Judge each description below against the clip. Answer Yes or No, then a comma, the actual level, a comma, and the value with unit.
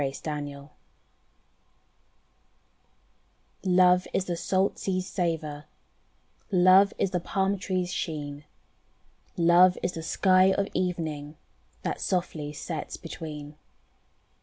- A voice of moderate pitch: Yes, medium, 175 Hz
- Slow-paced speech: Yes, slow, 100 wpm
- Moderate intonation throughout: Yes, average, 3.6 semitones